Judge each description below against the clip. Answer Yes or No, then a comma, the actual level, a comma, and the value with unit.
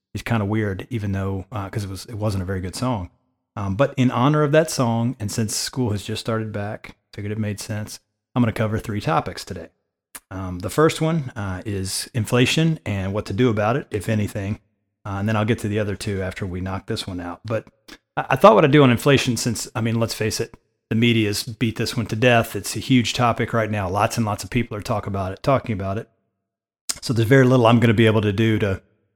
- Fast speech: Yes, fast, 255 wpm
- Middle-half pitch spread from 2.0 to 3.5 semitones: Yes, average, 2.8 semitones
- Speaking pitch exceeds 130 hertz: No, low, 110 Hz